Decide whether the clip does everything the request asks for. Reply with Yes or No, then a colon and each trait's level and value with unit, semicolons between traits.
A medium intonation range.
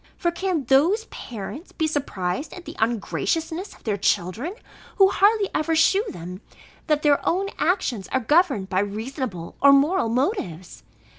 No: wide, 8.7 semitones